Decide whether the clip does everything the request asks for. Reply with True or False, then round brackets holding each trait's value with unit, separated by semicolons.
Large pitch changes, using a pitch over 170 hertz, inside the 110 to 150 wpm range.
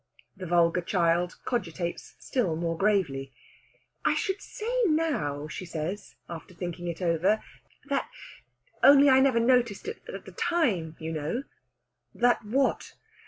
True (7.5 semitones; 185 Hz; 140 wpm)